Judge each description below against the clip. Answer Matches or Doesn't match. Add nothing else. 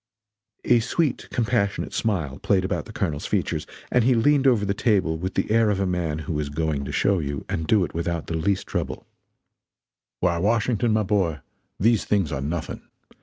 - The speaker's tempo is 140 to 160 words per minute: Doesn't match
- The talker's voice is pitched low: Matches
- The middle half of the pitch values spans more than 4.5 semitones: Matches